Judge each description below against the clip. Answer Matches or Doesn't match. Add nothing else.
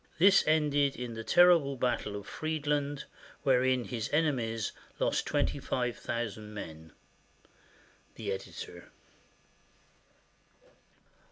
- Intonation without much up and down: Doesn't match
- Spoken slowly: Matches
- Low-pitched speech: Matches